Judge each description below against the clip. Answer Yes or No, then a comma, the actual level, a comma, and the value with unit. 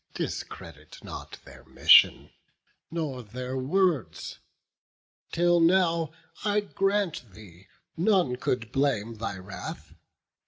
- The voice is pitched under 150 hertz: Yes, medium, 140 Hz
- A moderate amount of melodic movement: No, wide, 7.7 semitones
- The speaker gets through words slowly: Yes, slow, 95 wpm